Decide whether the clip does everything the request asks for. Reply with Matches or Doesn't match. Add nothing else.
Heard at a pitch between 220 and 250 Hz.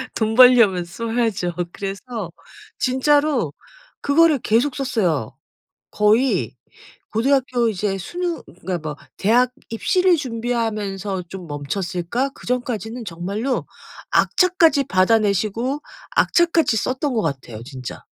Matches